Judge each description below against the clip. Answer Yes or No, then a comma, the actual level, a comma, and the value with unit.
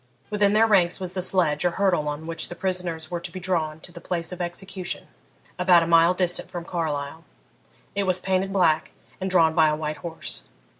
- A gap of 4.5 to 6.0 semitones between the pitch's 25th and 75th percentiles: No, narrow, 2.5 semitones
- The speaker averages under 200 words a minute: No, fast, 205 wpm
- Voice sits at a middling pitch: Yes, medium, 175 Hz